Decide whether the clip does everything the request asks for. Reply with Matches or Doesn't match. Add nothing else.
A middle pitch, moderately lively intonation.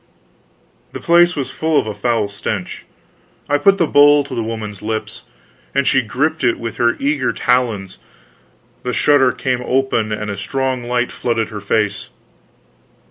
Doesn't match